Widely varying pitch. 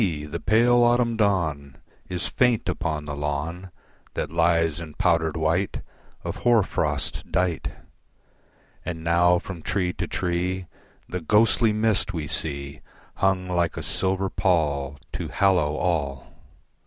No: average, 3.9 semitones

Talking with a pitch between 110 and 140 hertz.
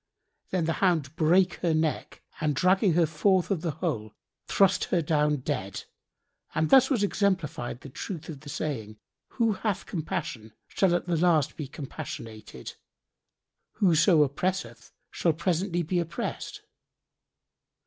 No: medium, 160 Hz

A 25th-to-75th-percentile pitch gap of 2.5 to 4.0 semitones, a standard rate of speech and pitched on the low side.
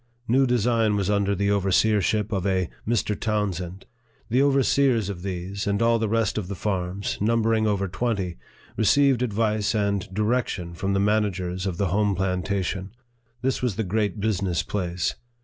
Yes: average, 2.8 semitones; average, 165 wpm; low, 100 Hz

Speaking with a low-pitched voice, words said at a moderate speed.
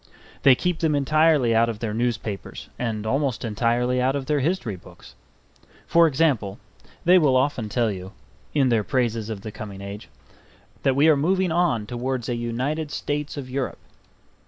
Yes: low, 125 Hz; average, 170 wpm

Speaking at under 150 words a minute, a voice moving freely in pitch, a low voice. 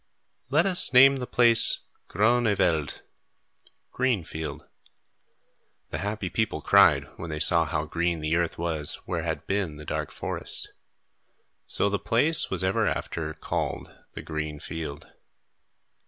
Yes: average, 140 wpm; wide, 6.5 semitones; very low, 90 Hz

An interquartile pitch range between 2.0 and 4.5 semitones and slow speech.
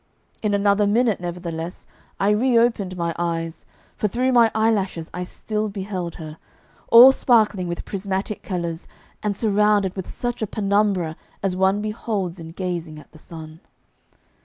No: average, 3.6 semitones; average, 145 wpm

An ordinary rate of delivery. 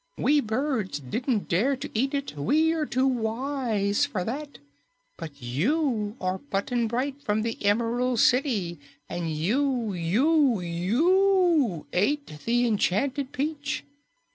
No: slow, 125 wpm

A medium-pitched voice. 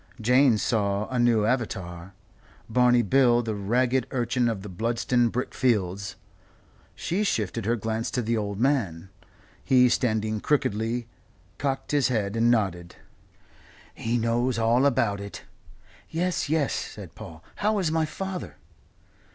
No: low, 115 Hz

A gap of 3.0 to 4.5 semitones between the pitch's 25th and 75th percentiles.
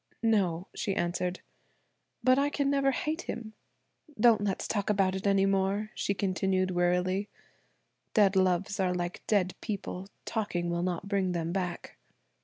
No: narrow, 2.5 semitones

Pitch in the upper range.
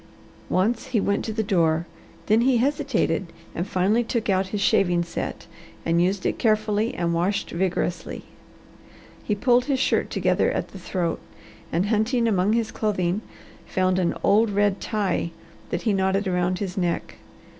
Yes: high, 200 Hz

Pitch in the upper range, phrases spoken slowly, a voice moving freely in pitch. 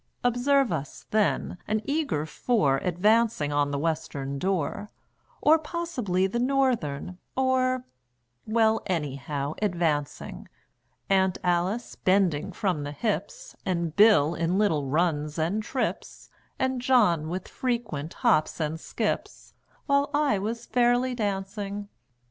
Yes: high, 195 Hz; slow, 120 wpm; wide, 7.3 semitones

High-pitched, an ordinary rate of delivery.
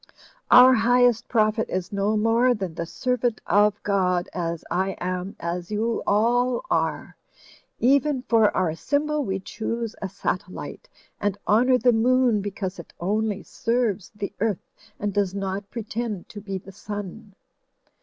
Yes: high, 210 Hz; average, 145 wpm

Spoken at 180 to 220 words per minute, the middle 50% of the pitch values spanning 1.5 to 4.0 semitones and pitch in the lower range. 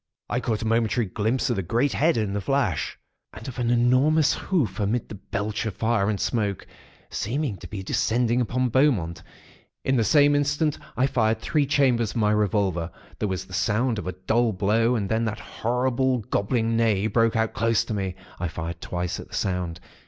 Yes: average, 195 wpm; average, 3.7 semitones; low, 115 Hz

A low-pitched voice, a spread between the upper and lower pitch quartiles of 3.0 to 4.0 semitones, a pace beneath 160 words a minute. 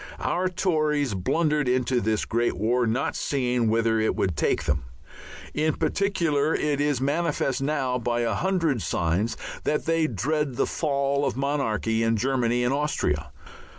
No: low, 130 Hz; average, 4.7 semitones; average, 150 wpm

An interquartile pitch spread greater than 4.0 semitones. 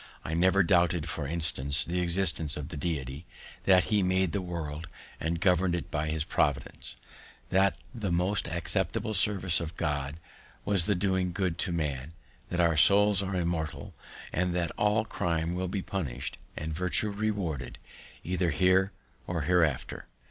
No: average, 3.0 semitones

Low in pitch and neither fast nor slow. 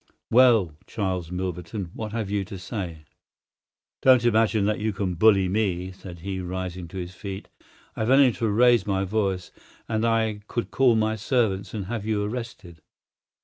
Yes: low, 100 Hz; average, 170 wpm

